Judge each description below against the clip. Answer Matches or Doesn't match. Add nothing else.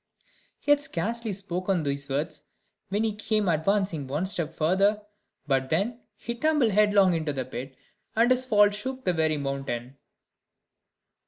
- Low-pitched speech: Doesn't match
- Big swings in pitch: Matches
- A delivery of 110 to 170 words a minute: Matches